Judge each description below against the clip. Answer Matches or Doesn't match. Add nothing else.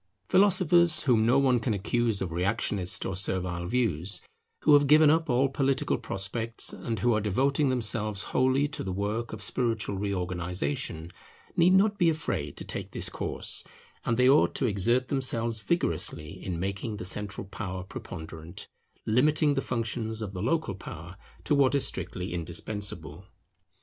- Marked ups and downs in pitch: Matches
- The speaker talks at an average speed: Matches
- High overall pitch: Doesn't match